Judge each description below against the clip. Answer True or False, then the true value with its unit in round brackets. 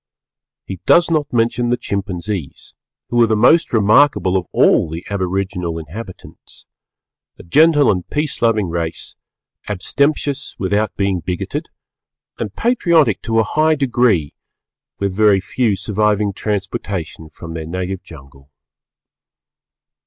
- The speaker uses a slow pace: True (120 wpm)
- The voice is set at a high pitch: False (100 Hz)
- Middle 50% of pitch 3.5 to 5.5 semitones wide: True (5.0 semitones)